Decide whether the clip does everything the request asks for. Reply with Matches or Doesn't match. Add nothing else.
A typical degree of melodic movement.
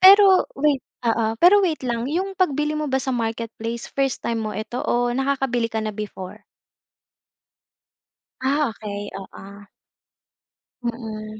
Matches